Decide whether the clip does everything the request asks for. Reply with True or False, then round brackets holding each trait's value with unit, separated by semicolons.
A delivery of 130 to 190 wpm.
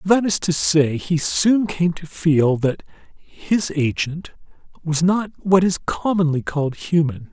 True (155 wpm)